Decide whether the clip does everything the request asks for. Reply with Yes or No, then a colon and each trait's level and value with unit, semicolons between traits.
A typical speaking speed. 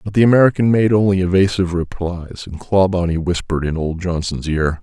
Yes: average, 175 wpm